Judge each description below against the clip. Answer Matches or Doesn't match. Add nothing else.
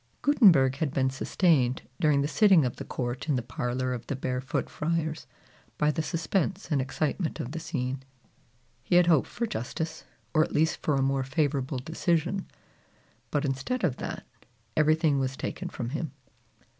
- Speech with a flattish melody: Doesn't match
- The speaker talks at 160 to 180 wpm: Matches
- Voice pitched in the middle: Matches